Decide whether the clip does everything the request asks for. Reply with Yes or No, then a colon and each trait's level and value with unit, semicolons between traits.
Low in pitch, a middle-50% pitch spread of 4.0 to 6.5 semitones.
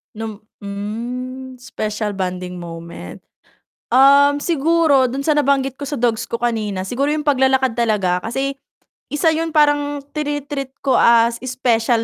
No: very high, 255 Hz; average, 4.4 semitones